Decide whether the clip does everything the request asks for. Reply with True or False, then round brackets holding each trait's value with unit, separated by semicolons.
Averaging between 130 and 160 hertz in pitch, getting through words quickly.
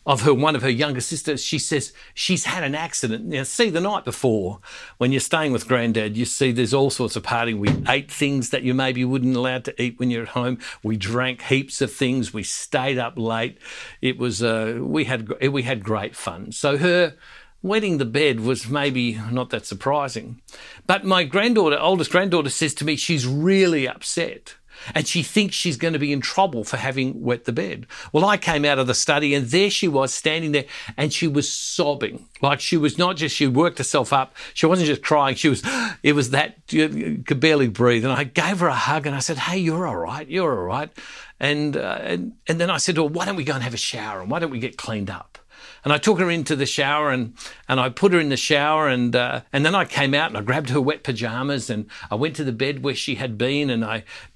True (140 Hz; 245 wpm)